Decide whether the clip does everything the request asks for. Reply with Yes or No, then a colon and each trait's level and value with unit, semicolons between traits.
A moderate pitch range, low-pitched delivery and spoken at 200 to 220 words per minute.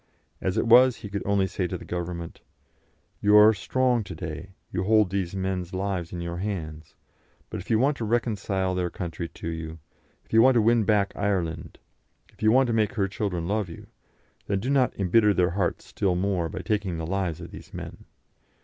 Yes: average, 3.6 semitones; very low, 95 Hz; fast, 205 wpm